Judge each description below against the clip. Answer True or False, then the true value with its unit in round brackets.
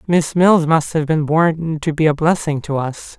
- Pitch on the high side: False (155 Hz)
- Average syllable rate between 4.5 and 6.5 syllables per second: False (4.3 syllables/s)